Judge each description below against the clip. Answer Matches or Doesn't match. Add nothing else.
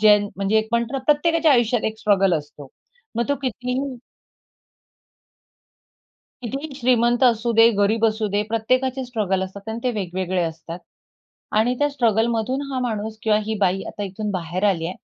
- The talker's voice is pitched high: Matches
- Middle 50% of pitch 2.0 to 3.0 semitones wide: Doesn't match